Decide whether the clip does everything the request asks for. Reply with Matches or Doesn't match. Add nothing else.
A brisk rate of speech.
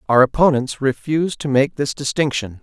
Doesn't match